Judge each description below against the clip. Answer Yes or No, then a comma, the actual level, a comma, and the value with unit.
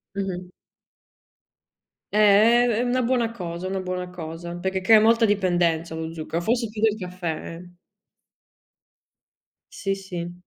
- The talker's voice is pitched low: No, medium, 185 Hz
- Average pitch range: Yes, average, 3.9 semitones